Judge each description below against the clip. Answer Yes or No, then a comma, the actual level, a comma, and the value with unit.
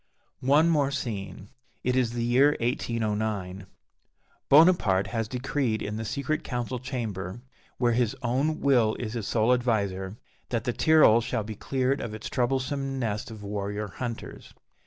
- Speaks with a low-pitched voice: Yes, low, 120 Hz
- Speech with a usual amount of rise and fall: Yes, average, 3.5 semitones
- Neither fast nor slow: Yes, average, 150 wpm